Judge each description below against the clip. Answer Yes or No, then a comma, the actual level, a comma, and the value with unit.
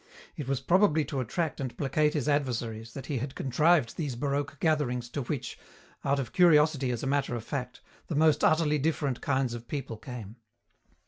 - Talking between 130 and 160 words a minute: No, average, 185 wpm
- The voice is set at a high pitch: No, medium, 140 Hz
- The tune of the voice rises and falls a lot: No, average, 3.4 semitones